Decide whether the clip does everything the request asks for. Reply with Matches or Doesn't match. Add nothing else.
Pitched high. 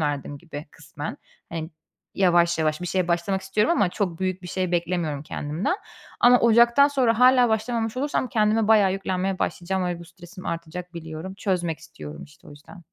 Doesn't match